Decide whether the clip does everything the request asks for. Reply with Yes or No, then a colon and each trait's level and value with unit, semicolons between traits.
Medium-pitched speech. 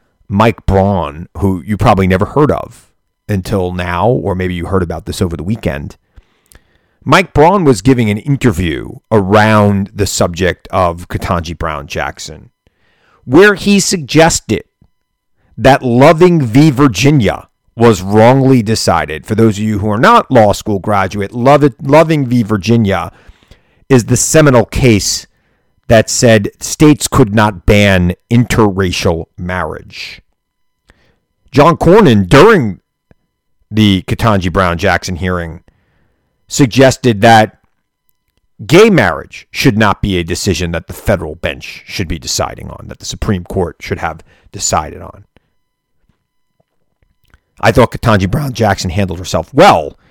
No: low, 105 Hz